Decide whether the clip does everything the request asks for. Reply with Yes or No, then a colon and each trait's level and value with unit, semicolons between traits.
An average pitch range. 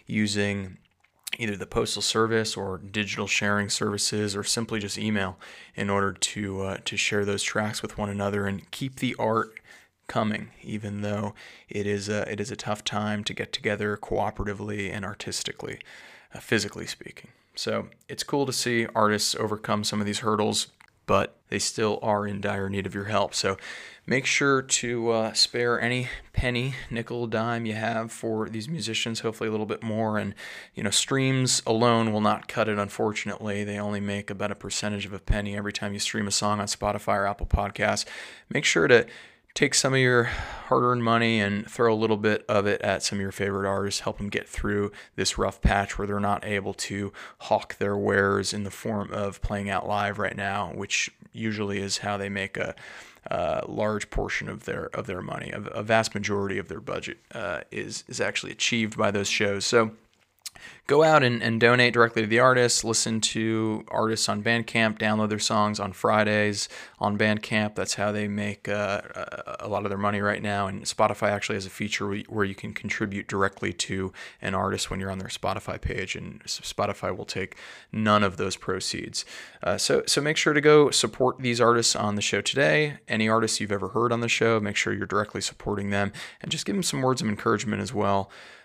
No: narrow, 1.8 semitones